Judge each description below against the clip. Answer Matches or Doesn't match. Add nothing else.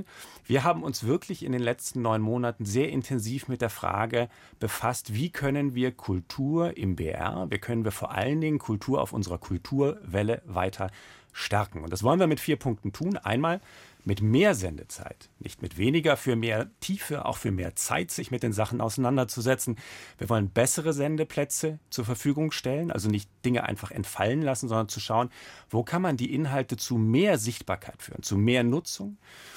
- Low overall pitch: Matches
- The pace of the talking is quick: Doesn't match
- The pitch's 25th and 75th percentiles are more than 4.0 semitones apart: Matches